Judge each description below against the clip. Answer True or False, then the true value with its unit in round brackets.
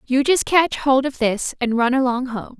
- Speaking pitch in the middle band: False (260 Hz)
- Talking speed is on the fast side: True (230 wpm)